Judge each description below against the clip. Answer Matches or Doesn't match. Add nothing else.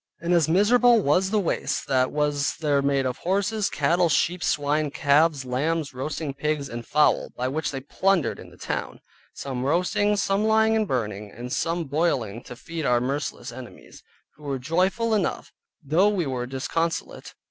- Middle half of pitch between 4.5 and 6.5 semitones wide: Matches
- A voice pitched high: Doesn't match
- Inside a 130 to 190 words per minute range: Matches